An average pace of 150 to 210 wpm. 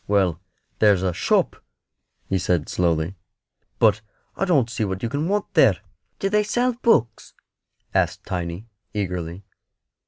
No: slow, 135 wpm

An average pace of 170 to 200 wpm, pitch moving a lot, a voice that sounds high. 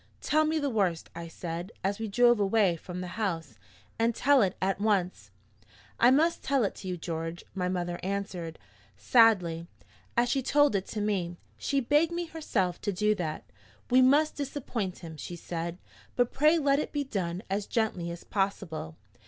Yes: average, 180 wpm; wide, 6.5 semitones; high, 200 Hz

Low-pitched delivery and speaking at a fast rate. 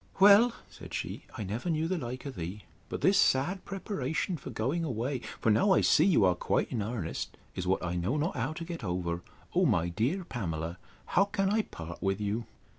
Yes: low, 125 Hz; fast, 210 wpm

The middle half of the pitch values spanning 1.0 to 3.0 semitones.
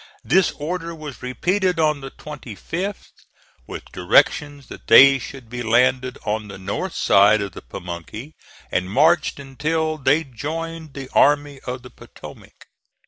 No: average, 4.6 semitones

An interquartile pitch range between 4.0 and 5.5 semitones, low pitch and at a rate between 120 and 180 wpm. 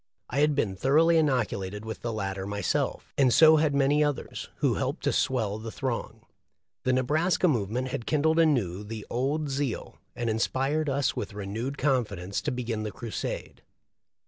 Yes: average, 5.2 semitones; low, 125 Hz; average, 170 wpm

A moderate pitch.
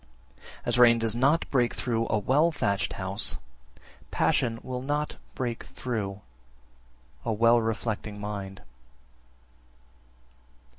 No: low, 115 Hz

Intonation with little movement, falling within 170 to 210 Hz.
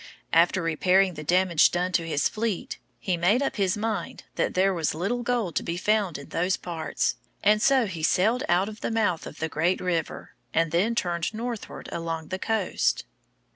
No: average, 4.2 semitones; medium, 185 Hz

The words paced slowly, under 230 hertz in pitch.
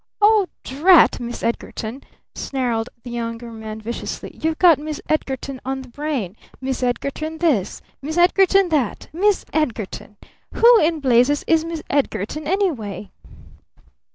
No: slow, 130 wpm; very high, 275 Hz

